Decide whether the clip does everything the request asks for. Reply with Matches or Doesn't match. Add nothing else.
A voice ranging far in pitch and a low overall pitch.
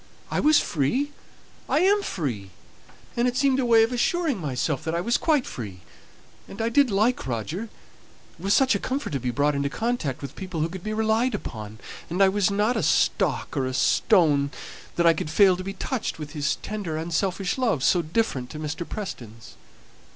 Doesn't match